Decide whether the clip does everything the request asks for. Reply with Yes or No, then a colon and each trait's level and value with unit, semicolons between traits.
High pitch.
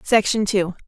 Yes: high, 200 Hz